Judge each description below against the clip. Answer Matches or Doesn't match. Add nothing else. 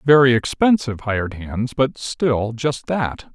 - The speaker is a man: Matches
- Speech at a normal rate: Matches